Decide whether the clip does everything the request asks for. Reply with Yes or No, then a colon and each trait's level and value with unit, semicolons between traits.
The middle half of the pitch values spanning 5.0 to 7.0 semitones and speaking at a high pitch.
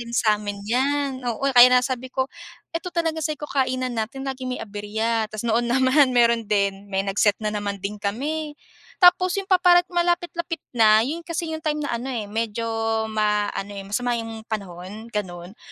Yes: wide, 5.5 semitones; high, 235 Hz